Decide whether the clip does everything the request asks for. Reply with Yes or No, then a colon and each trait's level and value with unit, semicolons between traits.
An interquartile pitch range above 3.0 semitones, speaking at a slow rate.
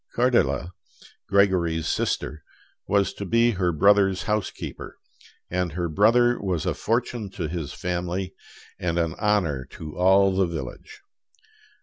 Yes: average, 3.4 semitones; slow, 125 wpm